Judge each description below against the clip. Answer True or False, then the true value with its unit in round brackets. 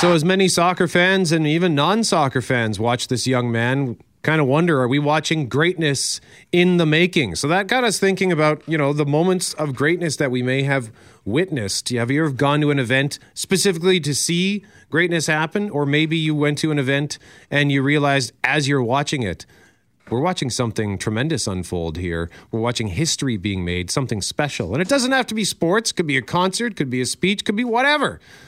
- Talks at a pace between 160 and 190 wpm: False (205 wpm)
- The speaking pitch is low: False (150 Hz)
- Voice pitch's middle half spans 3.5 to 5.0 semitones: False (5.6 semitones)